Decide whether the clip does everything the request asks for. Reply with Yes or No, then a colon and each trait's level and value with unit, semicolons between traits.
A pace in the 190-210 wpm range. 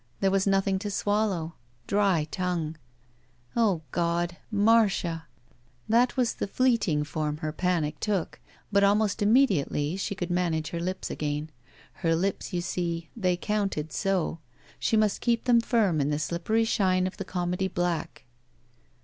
No: average, 150 wpm